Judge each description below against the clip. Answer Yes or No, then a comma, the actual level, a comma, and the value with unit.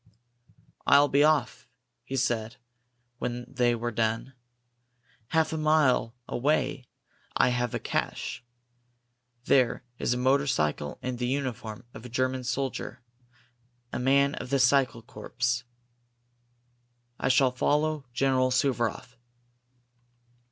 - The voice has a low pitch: Yes, low, 125 Hz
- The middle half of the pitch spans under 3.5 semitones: Yes, narrow, 2.4 semitones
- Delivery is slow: Yes, slow, 115 wpm